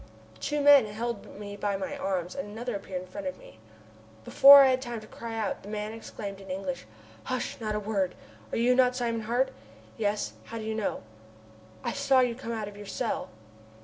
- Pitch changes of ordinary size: Yes, average, 3.6 semitones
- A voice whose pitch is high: Yes, high, 220 Hz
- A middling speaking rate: No, fast, 210 wpm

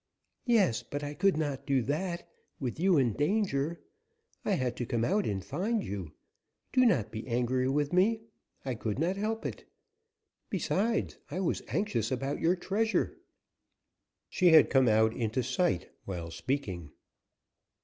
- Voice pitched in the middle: Yes, medium, 145 Hz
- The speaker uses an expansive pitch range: Yes, wide, 8.2 semitones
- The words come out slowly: No, average, 150 wpm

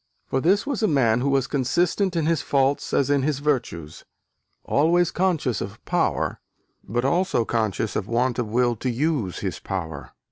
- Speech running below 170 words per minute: No, average, 175 wpm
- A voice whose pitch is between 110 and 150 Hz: Yes, low, 135 Hz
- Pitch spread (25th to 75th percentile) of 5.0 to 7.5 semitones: Yes, wide, 5.6 semitones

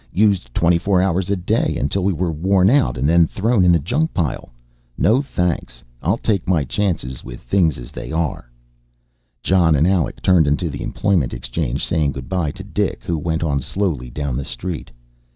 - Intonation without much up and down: No, average, 4.9 semitones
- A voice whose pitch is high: No, very low, 85 Hz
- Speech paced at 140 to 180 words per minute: No, average, 190 wpm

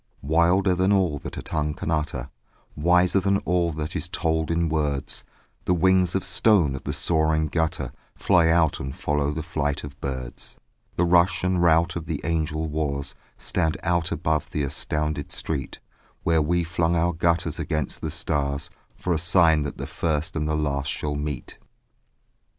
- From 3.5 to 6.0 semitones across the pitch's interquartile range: No, average, 2.7 semitones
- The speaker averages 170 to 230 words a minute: Yes, average, 175 wpm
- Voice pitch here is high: No, very low, 80 Hz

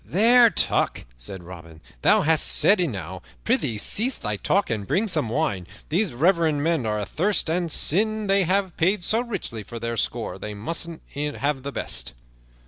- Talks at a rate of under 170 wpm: No, average, 175 wpm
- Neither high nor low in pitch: Yes, medium, 160 Hz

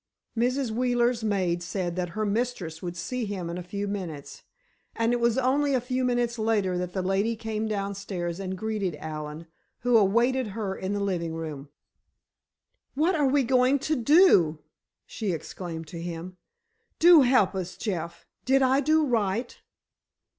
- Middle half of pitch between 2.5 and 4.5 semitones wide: No, wide, 5.6 semitones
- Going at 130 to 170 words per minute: Yes, average, 160 wpm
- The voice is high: Yes, high, 210 Hz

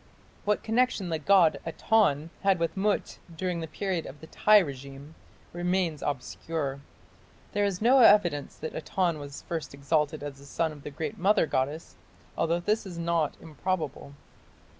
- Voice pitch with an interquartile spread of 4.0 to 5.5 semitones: Yes, average, 4.6 semitones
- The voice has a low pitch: No, medium, 165 Hz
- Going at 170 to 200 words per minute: No, average, 160 wpm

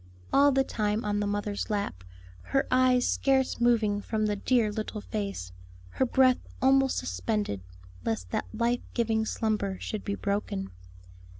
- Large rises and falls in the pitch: No, average, 3.4 semitones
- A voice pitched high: Yes, high, 215 Hz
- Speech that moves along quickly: No, average, 145 wpm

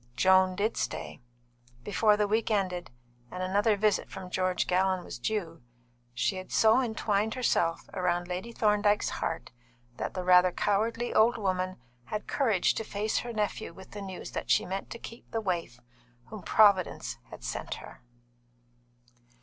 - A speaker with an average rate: Yes, average, 160 wpm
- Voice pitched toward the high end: Yes, high, 195 Hz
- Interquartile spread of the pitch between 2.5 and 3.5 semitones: Yes, average, 2.9 semitones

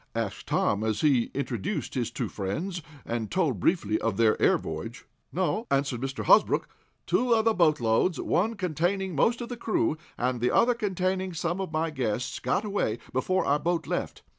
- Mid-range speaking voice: Yes, medium, 160 Hz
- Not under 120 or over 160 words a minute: No, average, 175 wpm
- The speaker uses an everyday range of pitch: No, wide, 7.7 semitones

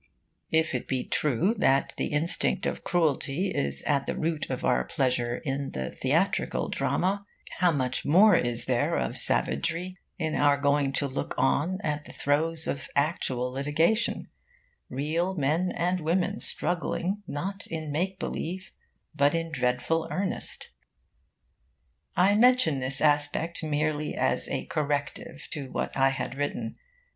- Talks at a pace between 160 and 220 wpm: No, average, 140 wpm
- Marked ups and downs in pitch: No, average, 4.3 semitones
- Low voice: No, medium, 150 Hz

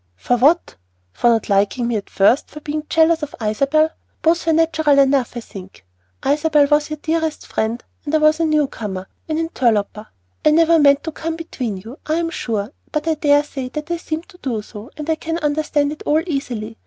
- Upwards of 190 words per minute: Yes, fast, 205 wpm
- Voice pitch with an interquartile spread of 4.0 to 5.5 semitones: Yes, average, 5.0 semitones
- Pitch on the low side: No, very high, 295 Hz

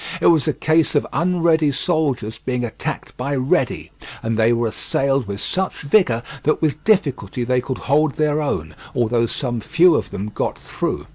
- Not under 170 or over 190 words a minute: Yes, average, 180 wpm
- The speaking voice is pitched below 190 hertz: Yes, medium, 140 Hz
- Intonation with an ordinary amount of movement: Yes, average, 4.9 semitones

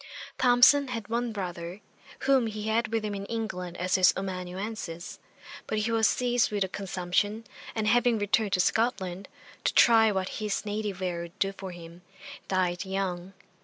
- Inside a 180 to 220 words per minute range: No, average, 165 wpm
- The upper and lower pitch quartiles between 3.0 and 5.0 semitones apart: Yes, average, 3.5 semitones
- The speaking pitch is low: No, high, 205 Hz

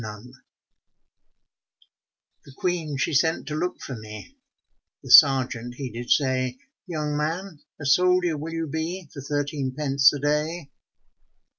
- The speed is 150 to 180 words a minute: No, slow, 135 wpm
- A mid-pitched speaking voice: Yes, medium, 145 Hz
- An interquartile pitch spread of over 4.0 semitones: No, average, 3.7 semitones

